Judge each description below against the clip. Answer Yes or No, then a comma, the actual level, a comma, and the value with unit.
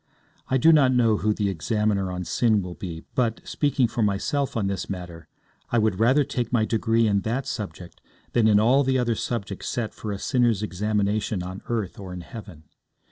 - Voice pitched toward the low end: Yes, low, 110 Hz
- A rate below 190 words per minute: No, average, 195 wpm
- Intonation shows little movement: No, average, 3.6 semitones